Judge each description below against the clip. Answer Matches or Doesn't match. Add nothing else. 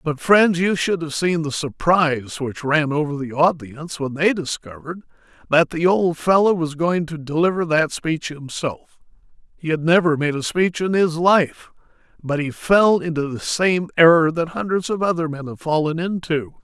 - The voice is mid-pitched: Matches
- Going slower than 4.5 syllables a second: Doesn't match